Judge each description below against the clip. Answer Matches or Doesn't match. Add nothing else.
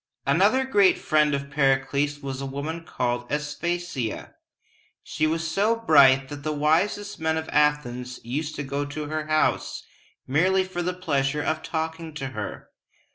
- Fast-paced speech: Doesn't match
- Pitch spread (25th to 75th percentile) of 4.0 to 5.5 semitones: Doesn't match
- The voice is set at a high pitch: Doesn't match